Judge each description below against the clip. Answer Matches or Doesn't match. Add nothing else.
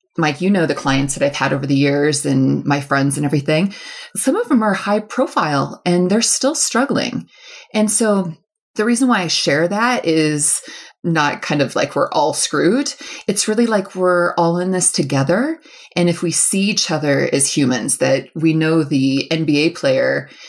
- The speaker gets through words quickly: Doesn't match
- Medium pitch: Matches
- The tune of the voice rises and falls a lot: Matches